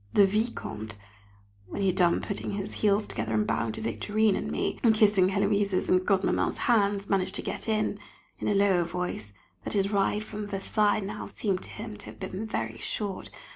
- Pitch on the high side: Yes, high, 200 Hz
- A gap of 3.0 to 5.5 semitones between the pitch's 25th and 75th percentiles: No, narrow, 2.4 semitones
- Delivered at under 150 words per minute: No, average, 195 wpm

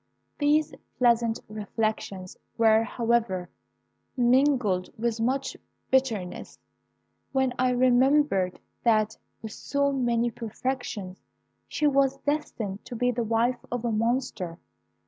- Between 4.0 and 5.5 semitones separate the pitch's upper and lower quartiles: No, average, 3.2 semitones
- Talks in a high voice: Yes, high, 235 Hz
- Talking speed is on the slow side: Yes, slow, 105 wpm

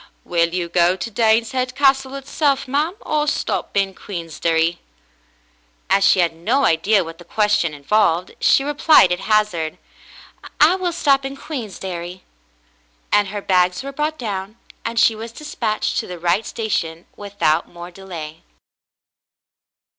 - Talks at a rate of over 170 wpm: No, average, 145 wpm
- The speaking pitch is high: Yes, high, 200 Hz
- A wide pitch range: Yes, wide, 7.2 semitones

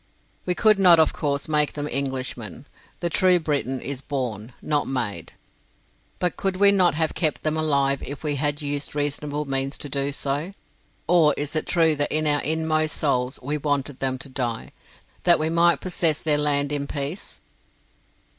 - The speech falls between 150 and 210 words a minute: Yes, average, 175 wpm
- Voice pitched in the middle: Yes, medium, 145 Hz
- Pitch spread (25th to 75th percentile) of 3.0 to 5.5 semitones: No, narrow, 2.5 semitones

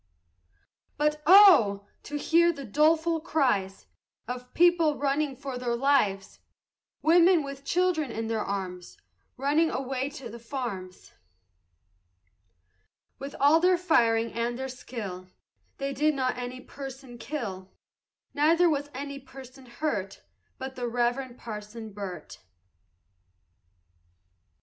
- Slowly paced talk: Yes, slow, 115 wpm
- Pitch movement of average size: Yes, average, 4.6 semitones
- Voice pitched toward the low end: No, very high, 265 Hz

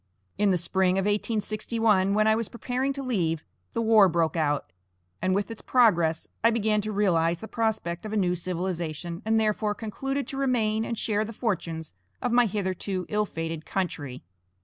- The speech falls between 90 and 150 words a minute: No, average, 180 wpm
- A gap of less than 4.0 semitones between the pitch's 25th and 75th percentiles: No, average, 4.4 semitones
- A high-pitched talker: Yes, high, 205 Hz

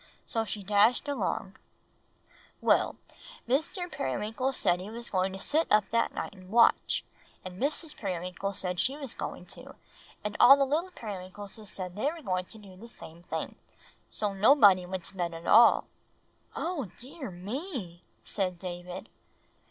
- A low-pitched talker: No, high, 205 Hz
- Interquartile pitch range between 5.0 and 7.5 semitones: Yes, wide, 5.6 semitones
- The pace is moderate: Yes, average, 160 wpm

